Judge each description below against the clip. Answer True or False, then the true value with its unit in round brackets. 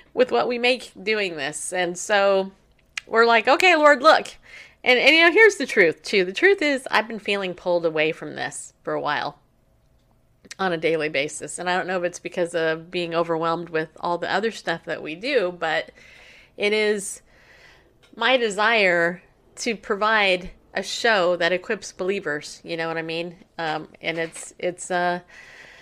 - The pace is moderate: True (180 wpm)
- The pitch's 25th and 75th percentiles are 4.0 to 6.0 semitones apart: True (4.9 semitones)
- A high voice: False (180 Hz)